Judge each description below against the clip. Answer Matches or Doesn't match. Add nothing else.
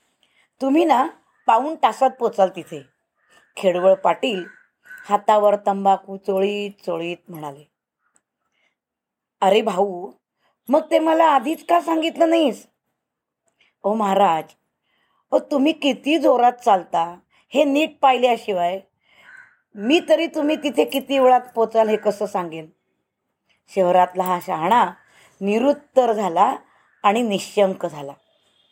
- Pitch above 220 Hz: Doesn't match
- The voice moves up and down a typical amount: Doesn't match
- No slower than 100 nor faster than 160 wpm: Matches